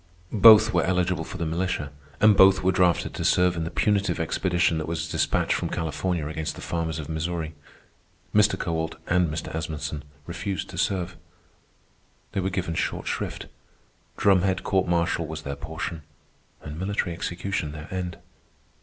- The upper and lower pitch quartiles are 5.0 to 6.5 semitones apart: No, average, 2.7 semitones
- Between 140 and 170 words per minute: Yes, average, 160 wpm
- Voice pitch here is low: Yes, very low, 85 Hz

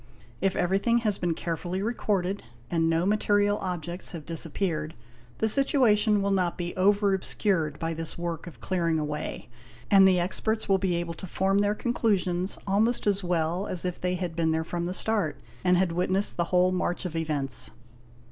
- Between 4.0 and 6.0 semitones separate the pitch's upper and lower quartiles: No, average, 3.0 semitones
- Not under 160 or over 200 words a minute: Yes, average, 185 wpm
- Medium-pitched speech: Yes, medium, 180 Hz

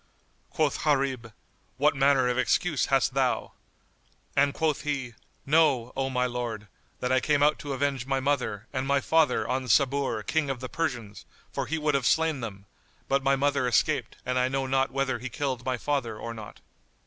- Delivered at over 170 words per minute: Yes, average, 185 wpm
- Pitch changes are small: Yes, narrow, 2.2 semitones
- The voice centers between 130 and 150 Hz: Yes, low, 135 Hz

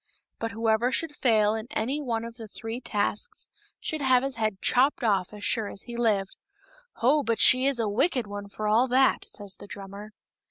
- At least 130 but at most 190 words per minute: No, fast, 205 wpm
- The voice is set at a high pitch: Yes, high, 230 Hz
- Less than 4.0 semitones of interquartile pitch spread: Yes, average, 3.5 semitones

